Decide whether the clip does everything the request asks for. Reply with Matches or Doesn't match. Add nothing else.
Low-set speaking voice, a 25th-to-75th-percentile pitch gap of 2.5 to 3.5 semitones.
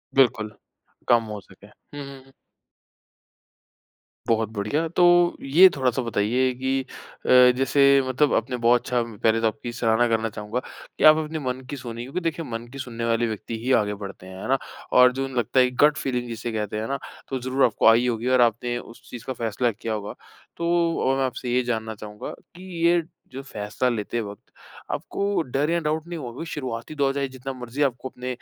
Matches